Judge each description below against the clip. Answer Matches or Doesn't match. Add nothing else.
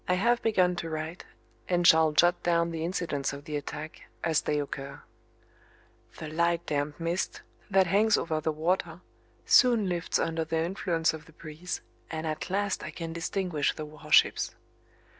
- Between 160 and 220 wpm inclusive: Matches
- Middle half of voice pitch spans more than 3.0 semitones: Doesn't match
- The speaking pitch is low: Doesn't match